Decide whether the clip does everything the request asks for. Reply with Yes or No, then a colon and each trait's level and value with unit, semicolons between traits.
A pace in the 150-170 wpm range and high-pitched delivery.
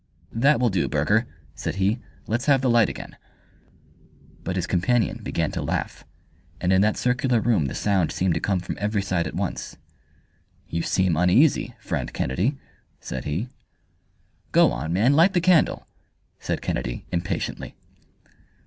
No: average, 155 wpm; low, 100 Hz